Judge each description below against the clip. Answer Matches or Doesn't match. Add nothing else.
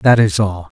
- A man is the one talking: Matches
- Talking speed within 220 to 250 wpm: Matches